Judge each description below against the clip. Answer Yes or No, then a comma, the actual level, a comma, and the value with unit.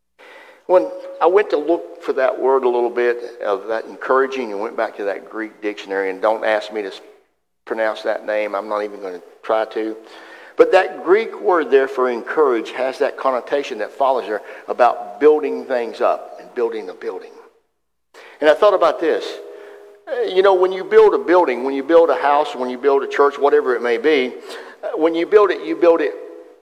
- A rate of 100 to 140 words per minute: No, fast, 205 wpm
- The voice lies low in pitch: No, high, 190 Hz